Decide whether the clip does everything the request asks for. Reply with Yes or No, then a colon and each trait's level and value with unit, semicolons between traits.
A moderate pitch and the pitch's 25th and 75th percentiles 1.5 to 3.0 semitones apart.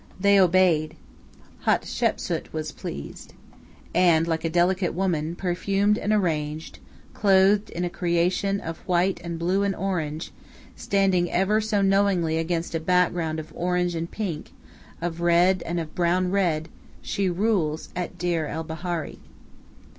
Yes: medium, 175 Hz; average, 2.7 semitones